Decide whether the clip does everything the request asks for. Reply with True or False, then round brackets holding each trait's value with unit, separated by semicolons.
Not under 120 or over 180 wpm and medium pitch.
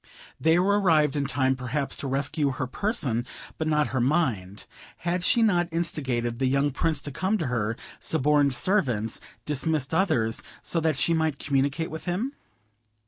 True (165 wpm; 145 Hz)